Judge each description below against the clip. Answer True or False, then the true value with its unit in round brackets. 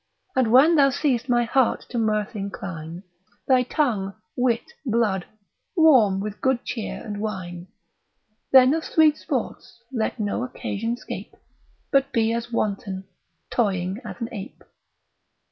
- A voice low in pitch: False (230 Hz)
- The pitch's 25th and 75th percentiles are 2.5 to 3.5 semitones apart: False (4.3 semitones)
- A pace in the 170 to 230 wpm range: False (135 wpm)